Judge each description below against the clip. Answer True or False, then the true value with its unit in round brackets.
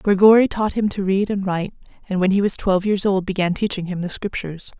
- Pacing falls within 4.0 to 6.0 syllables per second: False (6.2 syllables/s)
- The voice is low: False (195 Hz)